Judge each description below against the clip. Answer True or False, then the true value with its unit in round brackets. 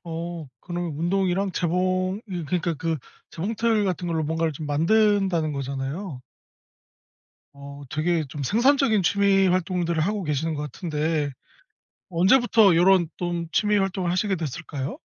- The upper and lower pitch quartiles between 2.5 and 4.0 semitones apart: True (3.6 semitones)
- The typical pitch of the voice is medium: True (175 Hz)